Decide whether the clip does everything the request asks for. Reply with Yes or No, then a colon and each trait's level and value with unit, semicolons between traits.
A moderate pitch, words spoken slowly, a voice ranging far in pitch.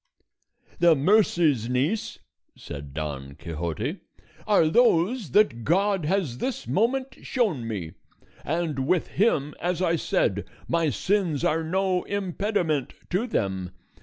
Yes: medium, 165 Hz; slow, 120 wpm; wide, 8.1 semitones